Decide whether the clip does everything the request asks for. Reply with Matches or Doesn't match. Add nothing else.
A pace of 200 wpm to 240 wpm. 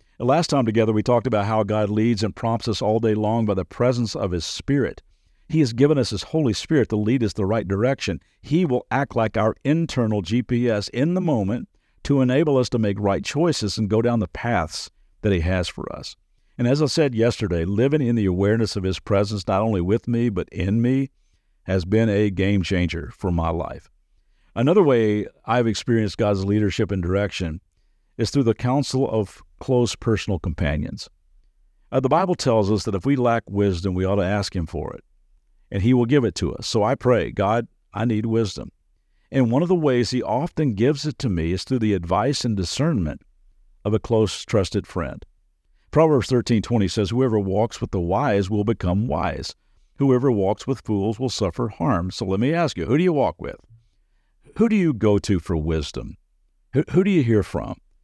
Matches